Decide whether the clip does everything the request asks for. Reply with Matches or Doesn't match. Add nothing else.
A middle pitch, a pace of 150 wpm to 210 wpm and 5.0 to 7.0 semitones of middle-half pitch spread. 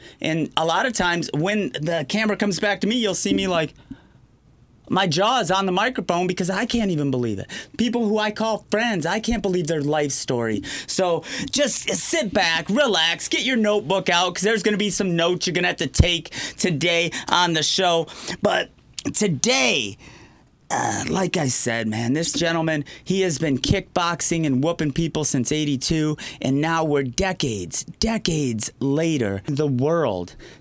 Matches